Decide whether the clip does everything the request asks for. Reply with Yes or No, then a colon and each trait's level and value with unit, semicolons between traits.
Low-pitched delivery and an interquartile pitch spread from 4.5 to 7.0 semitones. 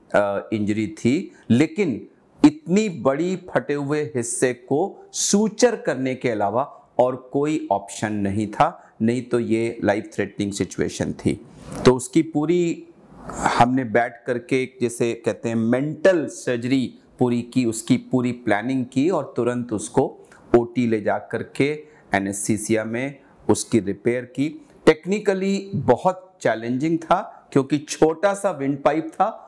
Yes: low, 130 Hz; average, 5.2 semitones